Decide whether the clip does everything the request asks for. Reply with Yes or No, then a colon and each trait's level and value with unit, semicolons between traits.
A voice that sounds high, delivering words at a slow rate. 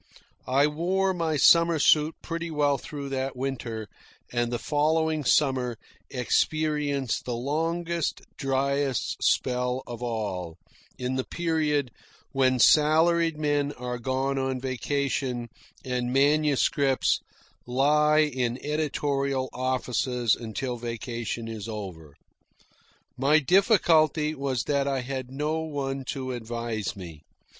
No: low, 135 Hz; slow, 115 wpm